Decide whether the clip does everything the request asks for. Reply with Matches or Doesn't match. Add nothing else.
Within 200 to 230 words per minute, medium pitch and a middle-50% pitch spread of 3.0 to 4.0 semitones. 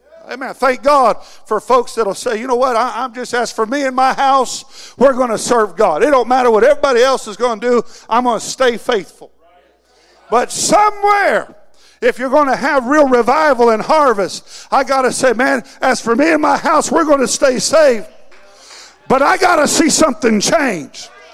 Doesn't match